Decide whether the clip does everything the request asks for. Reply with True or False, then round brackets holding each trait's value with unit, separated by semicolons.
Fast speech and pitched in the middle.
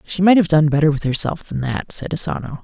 True (250 wpm; 155 Hz)